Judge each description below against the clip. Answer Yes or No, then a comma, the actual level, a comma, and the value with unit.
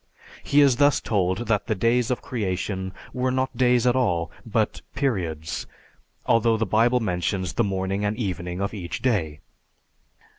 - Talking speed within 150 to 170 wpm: Yes, average, 155 wpm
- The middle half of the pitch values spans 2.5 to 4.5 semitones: No, average, 4.9 semitones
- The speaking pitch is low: Yes, low, 110 Hz